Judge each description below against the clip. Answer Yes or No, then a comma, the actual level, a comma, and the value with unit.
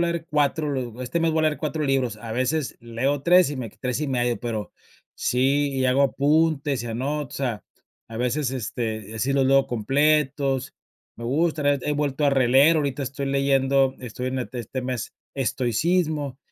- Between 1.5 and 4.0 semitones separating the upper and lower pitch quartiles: Yes, average, 2.9 semitones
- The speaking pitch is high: No, low, 135 Hz